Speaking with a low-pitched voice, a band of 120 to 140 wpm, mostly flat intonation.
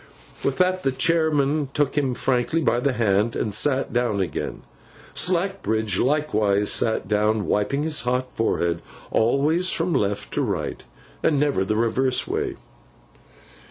No: low, 130 Hz; slow, 135 wpm; wide, 5.5 semitones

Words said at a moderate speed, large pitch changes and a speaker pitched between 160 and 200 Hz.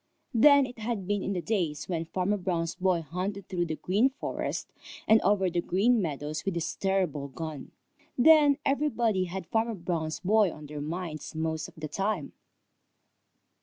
No: average, 165 wpm; average, 5.0 semitones; medium, 185 Hz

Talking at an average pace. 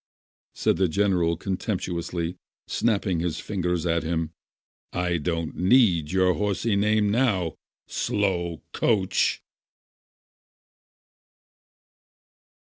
No: slow, 85 wpm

